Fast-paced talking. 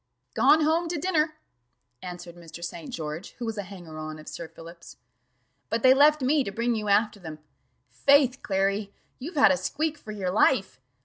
No: average, 185 wpm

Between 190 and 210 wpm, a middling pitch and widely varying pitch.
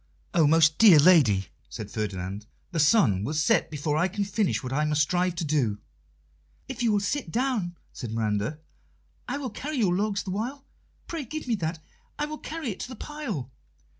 Yes: average, 195 wpm; medium, 175 Hz; wide, 7.9 semitones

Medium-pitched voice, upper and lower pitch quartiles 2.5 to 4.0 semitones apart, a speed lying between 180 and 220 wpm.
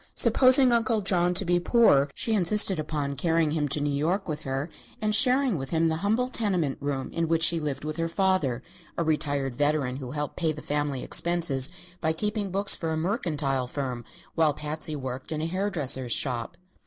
No: medium, 160 Hz; average, 4.8 semitones; average, 195 wpm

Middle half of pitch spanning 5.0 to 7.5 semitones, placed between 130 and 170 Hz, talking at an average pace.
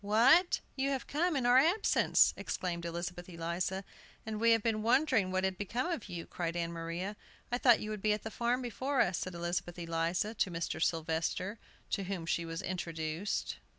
No: wide, 5.5 semitones; high, 190 Hz; average, 190 wpm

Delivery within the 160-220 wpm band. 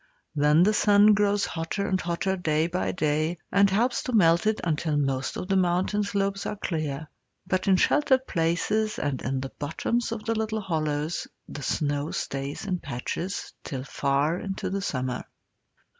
Yes: average, 170 wpm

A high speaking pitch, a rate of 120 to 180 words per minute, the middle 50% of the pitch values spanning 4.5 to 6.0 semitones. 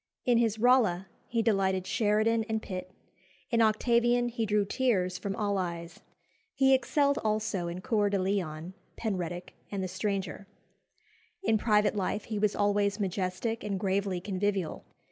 No: high, 205 Hz; average, 145 wpm; average, 3.0 semitones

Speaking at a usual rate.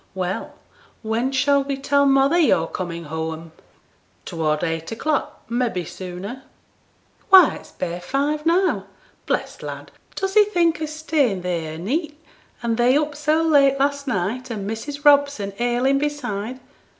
Yes: average, 150 wpm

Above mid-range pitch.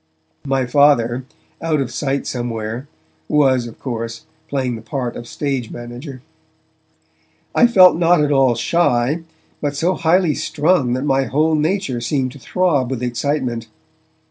No: low, 135 Hz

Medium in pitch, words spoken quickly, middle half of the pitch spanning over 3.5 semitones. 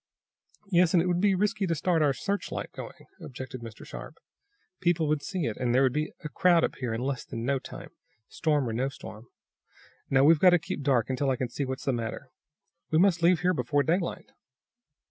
Yes: medium, 145 Hz; fast, 210 wpm; average, 5.2 semitones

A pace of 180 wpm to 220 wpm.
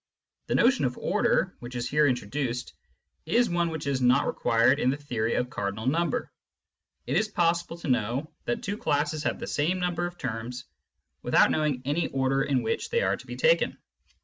Yes: average, 190 wpm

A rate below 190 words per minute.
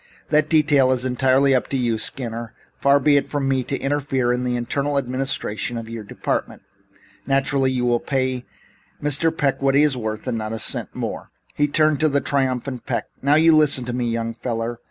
No: average, 200 wpm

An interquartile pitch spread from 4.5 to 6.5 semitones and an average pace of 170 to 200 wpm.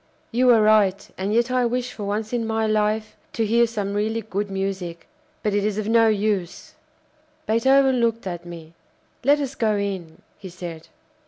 No: average, 2.8 semitones; average, 180 wpm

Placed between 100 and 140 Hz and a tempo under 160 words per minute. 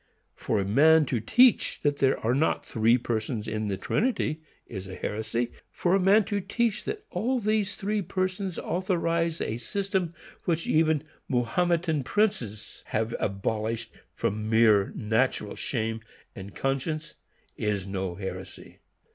Yes: low, 135 Hz; average, 140 wpm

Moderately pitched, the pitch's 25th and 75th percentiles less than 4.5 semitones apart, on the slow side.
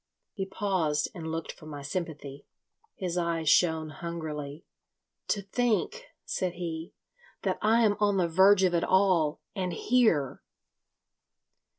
Yes: medium, 170 Hz; average, 3.3 semitones; slow, 130 wpm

